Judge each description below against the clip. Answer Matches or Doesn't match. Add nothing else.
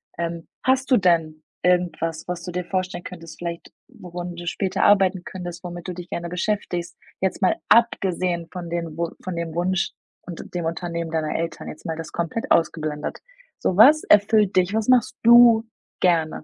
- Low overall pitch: Doesn't match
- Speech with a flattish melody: Matches